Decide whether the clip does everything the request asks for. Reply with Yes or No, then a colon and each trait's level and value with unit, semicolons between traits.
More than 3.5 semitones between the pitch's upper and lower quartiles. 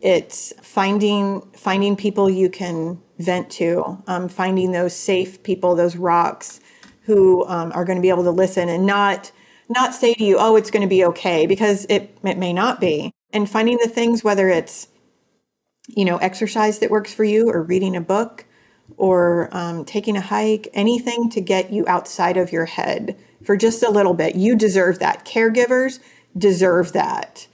No: average, 3.1 semitones